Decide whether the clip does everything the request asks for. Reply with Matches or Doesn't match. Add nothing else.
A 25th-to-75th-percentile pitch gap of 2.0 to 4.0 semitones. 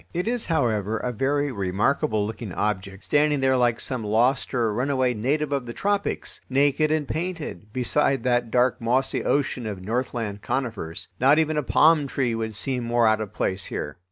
Doesn't match